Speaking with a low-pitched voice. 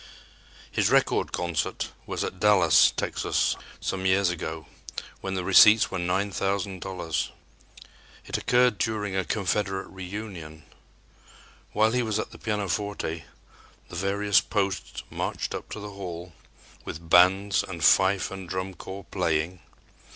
Yes: very low, 95 Hz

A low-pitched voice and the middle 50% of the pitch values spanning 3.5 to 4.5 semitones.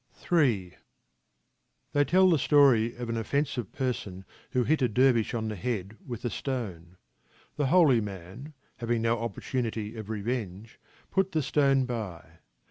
Yes: low, 120 Hz; average, 4.2 semitones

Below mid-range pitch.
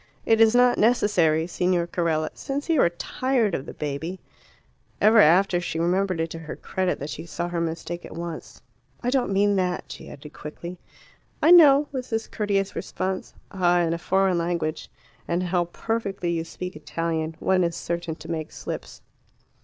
No: medium, 175 Hz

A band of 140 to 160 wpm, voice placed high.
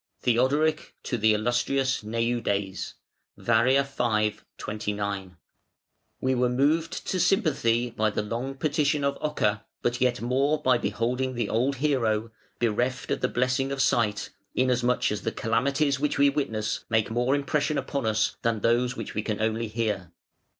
No: average, 150 wpm; low, 120 Hz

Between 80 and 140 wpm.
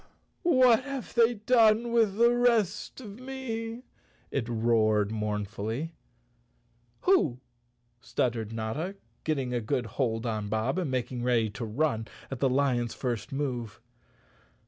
Yes: slow, 135 wpm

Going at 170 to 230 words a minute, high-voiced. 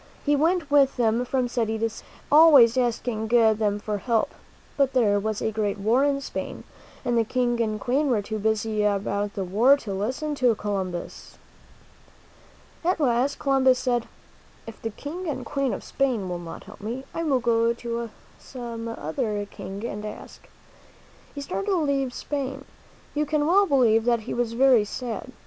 Yes: average, 175 wpm; high, 235 Hz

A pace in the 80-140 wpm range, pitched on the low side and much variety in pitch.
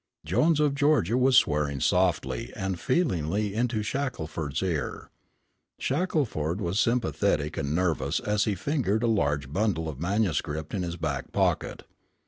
Yes: slow, 135 wpm; very low, 95 Hz; wide, 7.5 semitones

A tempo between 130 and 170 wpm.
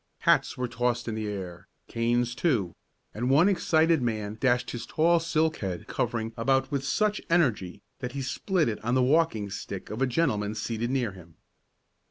No: average, 180 wpm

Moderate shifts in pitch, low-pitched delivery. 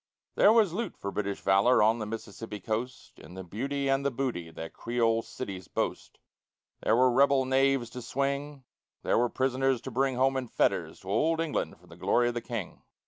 Yes: average, 3.9 semitones; low, 125 Hz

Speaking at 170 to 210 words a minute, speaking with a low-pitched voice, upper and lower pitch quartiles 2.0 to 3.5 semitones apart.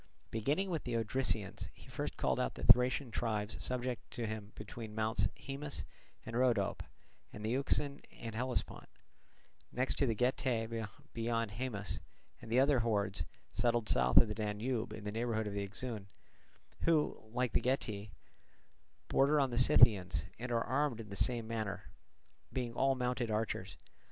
No: average, 155 wpm; low, 115 Hz; average, 3.0 semitones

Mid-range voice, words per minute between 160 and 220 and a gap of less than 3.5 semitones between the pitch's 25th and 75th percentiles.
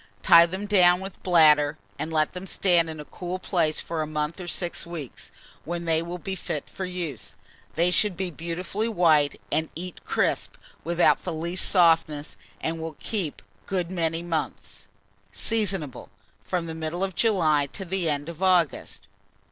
Yes: medium, 170 Hz; average, 170 wpm; narrow, 2.5 semitones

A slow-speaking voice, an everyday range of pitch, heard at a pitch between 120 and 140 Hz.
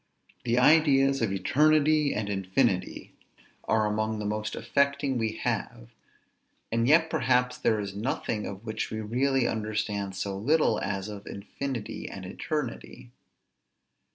No: slow, 130 wpm; average, 4.8 semitones; low, 110 Hz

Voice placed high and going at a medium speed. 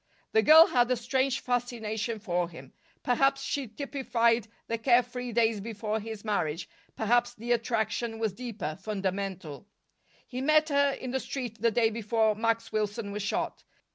Yes: high, 230 Hz; average, 160 wpm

